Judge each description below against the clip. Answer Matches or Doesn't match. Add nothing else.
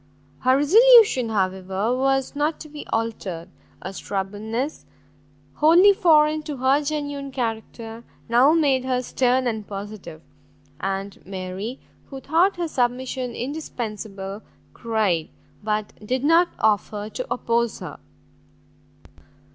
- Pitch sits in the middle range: Doesn't match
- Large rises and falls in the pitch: Matches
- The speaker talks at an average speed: Doesn't match